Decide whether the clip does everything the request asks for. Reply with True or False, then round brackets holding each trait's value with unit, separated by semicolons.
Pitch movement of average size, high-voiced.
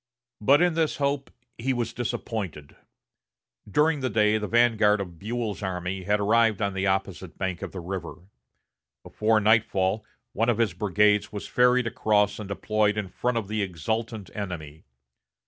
False (3.2 semitones; 105 Hz)